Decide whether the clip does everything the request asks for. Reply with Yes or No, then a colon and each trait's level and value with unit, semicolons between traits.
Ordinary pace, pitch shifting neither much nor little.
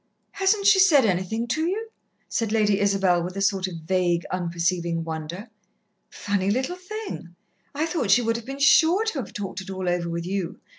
No: average, 190 wpm; wide, 7.9 semitones